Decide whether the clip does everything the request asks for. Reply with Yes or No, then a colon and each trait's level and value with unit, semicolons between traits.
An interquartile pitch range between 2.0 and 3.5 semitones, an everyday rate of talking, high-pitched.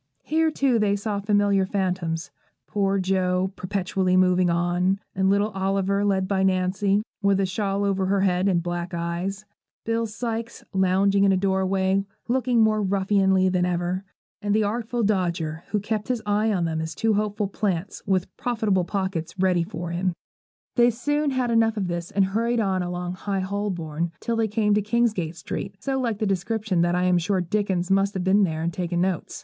Yes: narrow, 2.4 semitones; average, 190 wpm; high, 195 Hz